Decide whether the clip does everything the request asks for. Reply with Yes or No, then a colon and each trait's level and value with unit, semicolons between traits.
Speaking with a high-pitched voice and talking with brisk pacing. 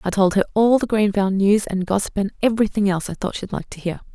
Yes: high, 200 Hz; fast, 260 wpm